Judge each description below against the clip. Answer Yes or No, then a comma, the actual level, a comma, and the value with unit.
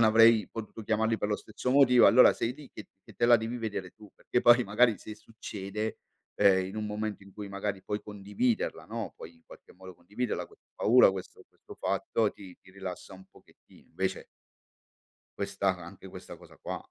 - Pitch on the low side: Yes, low, 105 Hz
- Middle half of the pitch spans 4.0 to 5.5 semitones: No, average, 2.7 semitones